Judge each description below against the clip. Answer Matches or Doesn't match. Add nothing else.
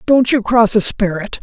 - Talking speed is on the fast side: Matches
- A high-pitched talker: Matches